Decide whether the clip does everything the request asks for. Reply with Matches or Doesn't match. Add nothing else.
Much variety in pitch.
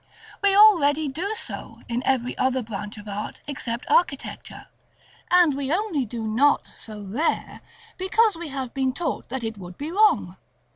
Matches